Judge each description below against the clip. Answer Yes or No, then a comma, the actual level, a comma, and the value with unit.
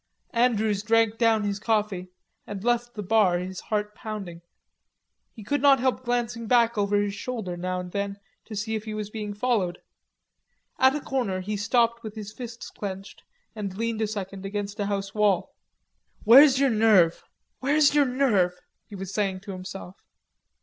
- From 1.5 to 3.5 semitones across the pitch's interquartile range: Yes, average, 2.9 semitones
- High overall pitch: Yes, high, 210 Hz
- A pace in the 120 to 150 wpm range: No, average, 170 wpm